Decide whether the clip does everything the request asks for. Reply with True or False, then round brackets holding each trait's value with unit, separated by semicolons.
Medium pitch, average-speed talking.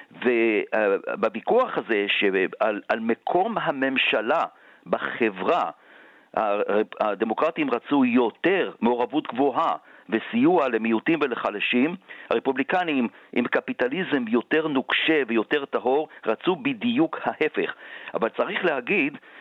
False (150 Hz; 85 wpm)